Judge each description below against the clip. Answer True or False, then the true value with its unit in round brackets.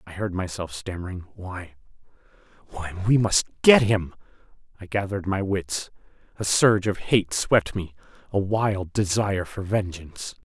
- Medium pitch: False (95 Hz)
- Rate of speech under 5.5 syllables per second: True (4.7 syllables/s)